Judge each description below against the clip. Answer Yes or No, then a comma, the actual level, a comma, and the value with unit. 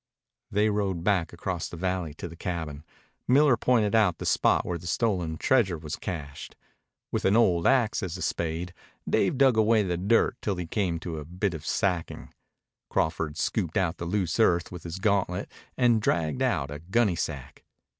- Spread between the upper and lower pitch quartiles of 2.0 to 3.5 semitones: No, average, 4.1 semitones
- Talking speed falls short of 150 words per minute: No, average, 180 wpm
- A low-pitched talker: Yes, very low, 90 Hz